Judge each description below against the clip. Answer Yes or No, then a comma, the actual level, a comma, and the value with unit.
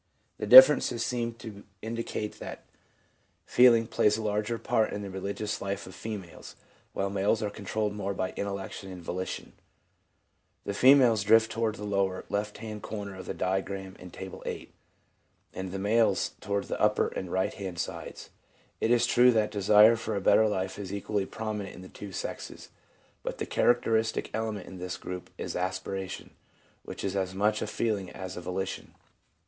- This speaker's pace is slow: No, average, 175 wpm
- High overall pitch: No, low, 100 Hz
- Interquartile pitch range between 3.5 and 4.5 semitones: No, narrow, 2.6 semitones